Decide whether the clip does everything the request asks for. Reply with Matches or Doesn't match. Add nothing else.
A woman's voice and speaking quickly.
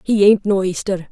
Matches